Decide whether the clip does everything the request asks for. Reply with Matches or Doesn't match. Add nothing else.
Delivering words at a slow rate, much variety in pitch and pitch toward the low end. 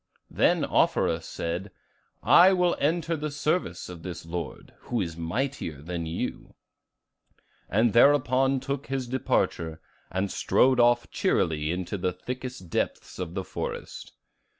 Matches